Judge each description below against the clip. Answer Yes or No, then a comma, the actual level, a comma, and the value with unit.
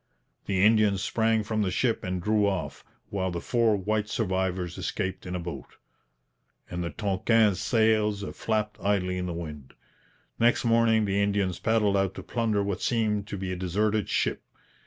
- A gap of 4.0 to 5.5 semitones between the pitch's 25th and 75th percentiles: No, average, 2.7 semitones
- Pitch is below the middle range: Yes, low, 100 Hz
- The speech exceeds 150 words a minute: Yes, average, 170 wpm